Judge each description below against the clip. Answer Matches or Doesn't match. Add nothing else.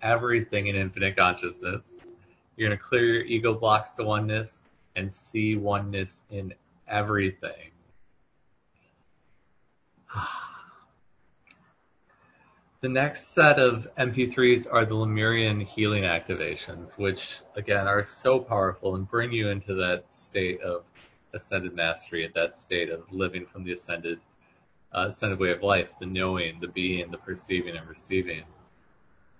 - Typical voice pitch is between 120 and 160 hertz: Doesn't match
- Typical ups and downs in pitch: Matches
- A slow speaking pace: Matches